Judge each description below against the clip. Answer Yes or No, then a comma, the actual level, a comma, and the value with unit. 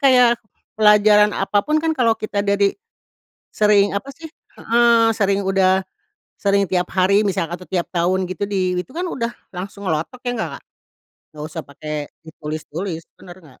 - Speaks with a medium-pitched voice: No, high, 200 Hz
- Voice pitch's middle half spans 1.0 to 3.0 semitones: No, average, 3.6 semitones